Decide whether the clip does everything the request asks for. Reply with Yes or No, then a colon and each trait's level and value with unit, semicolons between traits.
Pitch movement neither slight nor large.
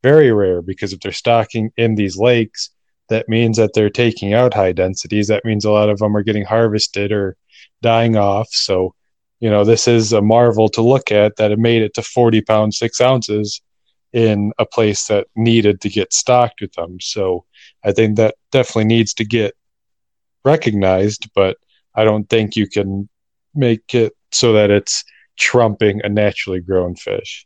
No: narrow, 2.0 semitones